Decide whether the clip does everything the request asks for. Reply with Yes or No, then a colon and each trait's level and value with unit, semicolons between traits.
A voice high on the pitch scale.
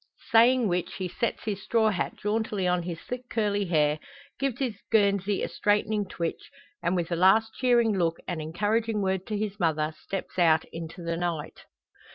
Yes: high, 195 Hz